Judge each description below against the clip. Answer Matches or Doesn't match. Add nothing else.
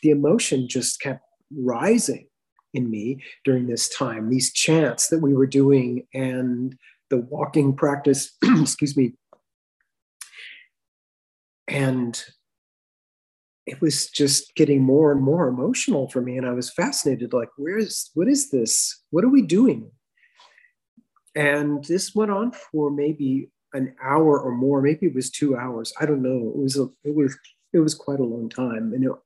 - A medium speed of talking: Matches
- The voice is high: Doesn't match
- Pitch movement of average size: Matches